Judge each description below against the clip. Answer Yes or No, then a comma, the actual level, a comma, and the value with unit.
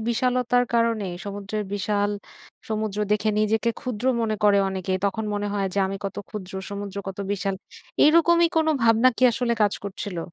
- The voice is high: Yes, high, 210 Hz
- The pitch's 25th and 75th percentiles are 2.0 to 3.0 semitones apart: Yes, average, 2.7 semitones